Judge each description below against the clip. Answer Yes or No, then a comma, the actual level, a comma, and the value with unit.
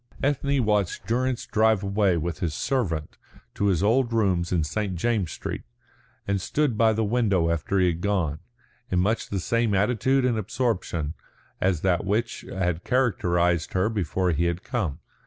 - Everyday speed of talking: Yes, average, 165 wpm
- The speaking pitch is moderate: No, low, 100 Hz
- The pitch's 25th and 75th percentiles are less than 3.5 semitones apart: No, average, 4.7 semitones